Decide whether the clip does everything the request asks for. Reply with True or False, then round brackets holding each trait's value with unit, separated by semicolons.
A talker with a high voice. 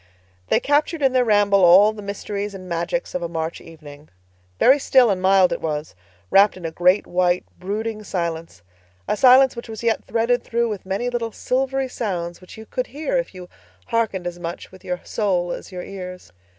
True (195 Hz)